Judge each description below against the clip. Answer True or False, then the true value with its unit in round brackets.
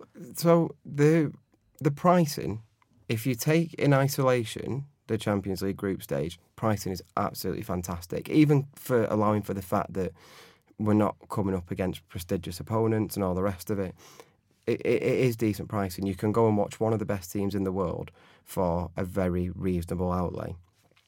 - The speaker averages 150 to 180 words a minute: True (175 wpm)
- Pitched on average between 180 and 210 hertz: False (105 Hz)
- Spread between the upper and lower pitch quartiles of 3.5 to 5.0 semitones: True (4.0 semitones)